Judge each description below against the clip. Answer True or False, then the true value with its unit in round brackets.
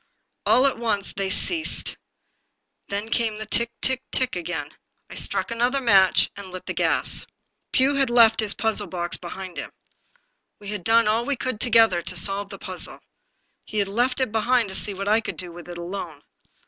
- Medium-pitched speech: False (210 Hz)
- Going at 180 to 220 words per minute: True (190 wpm)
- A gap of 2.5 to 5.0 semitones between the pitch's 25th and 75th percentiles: True (3.8 semitones)